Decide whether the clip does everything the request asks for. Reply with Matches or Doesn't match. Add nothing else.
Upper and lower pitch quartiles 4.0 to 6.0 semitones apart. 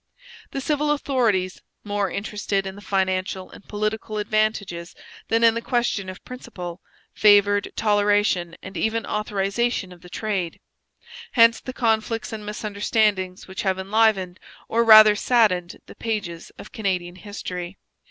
Doesn't match